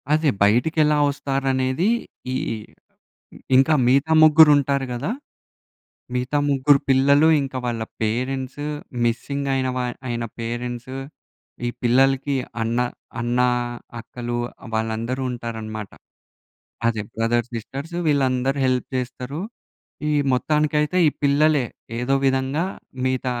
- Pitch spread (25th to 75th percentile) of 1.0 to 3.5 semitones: Yes, average, 2.9 semitones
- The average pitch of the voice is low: Yes, low, 130 Hz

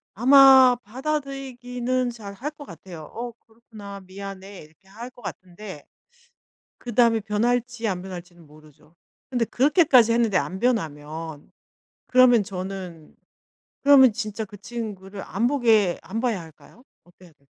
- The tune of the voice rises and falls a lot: No, average, 4.8 semitones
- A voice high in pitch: Yes, high, 215 Hz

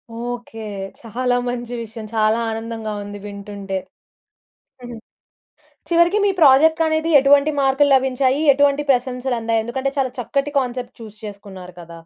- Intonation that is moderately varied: Yes, average, 3.7 semitones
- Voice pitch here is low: No, high, 245 Hz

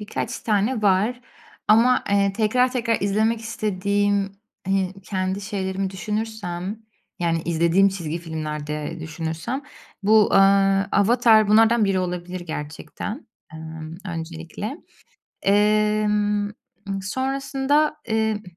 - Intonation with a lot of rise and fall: No, average, 3.9 semitones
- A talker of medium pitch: No, high, 200 Hz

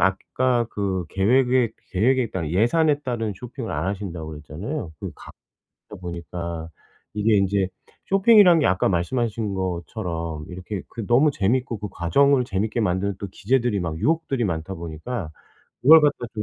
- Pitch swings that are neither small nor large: No, wide, 6.0 semitones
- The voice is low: Yes, low, 105 Hz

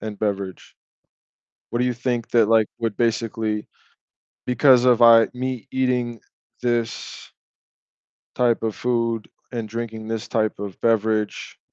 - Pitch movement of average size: No, narrow, 1.8 semitones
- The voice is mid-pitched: No, low, 115 Hz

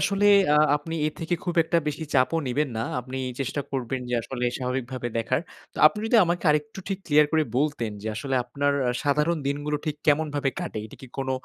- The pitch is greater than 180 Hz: No, medium, 145 Hz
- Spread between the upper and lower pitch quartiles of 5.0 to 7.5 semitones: No, average, 2.9 semitones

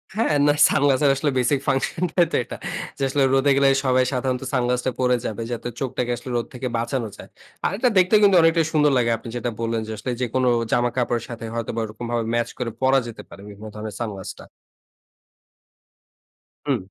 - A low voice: Yes, low, 125 Hz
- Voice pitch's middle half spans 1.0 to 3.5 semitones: Yes, average, 2.9 semitones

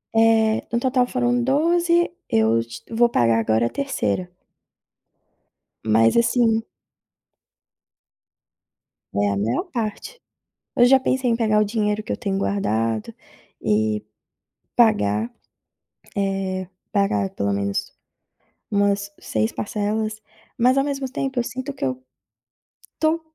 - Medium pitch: No, high, 215 Hz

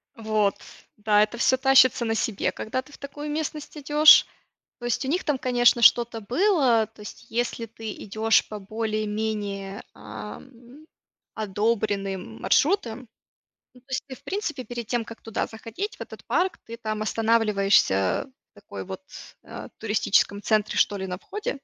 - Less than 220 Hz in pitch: No, high, 225 Hz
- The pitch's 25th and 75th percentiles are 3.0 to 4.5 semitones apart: Yes, average, 3.7 semitones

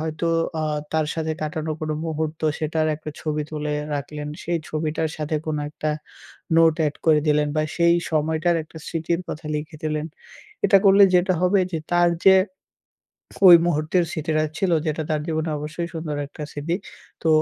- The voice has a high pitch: No, medium, 155 Hz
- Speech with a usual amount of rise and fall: No, narrow, 1.8 semitones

